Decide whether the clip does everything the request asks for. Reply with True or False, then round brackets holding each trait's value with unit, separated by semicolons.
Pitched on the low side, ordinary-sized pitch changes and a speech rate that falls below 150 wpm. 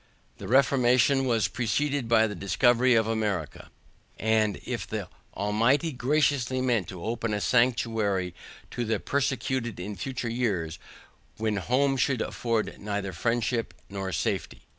True (115 Hz; 3.5 semitones; 135 wpm)